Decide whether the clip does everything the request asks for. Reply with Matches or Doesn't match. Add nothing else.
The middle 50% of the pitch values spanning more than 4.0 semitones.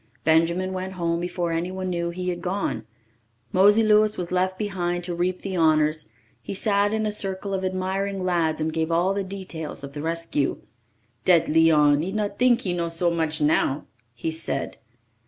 Doesn't match